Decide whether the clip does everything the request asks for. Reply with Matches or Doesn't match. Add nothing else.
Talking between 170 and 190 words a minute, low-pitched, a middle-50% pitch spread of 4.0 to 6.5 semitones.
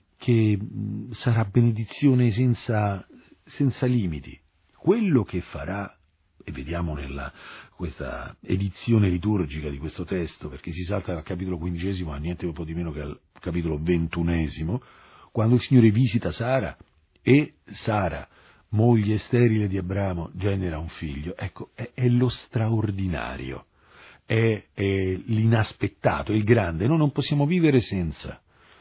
Doesn't match